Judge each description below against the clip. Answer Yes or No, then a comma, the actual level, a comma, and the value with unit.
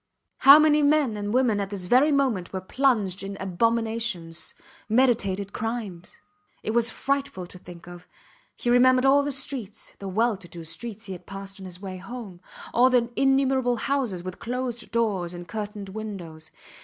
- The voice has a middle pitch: No, high, 220 Hz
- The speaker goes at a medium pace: Yes, average, 170 wpm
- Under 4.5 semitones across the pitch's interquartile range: No, average, 5.0 semitones